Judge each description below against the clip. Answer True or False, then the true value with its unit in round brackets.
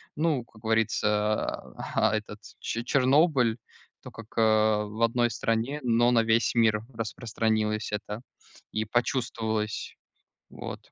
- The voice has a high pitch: False (115 Hz)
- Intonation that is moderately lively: False (1.9 semitones)